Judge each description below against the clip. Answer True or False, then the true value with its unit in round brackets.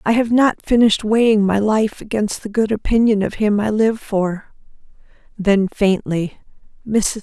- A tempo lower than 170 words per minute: True (150 wpm)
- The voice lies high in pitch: True (210 Hz)